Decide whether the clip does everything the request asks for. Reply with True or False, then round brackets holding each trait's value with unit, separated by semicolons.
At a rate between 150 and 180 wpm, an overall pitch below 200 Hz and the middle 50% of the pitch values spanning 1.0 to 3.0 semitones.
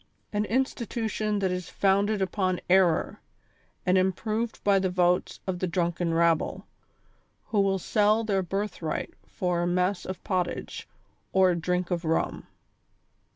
False (140 wpm; 185 Hz; 2.4 semitones)